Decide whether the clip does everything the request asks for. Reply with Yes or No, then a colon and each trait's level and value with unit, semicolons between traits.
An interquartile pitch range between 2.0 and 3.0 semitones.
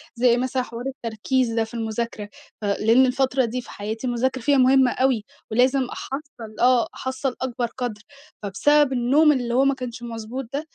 Yes: narrow, 2.4 semitones